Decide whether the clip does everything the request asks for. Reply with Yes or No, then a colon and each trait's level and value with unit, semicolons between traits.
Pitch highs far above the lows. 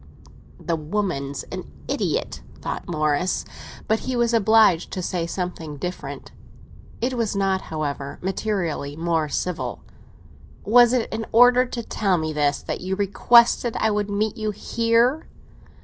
Yes: wide, 5.7 semitones